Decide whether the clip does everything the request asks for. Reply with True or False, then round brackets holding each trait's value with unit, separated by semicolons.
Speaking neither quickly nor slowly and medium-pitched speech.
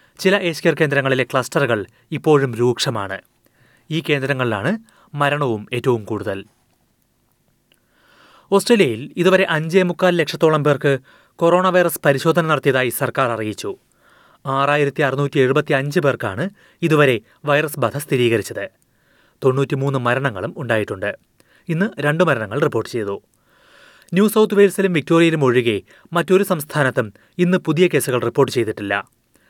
True (105 wpm; 145 Hz)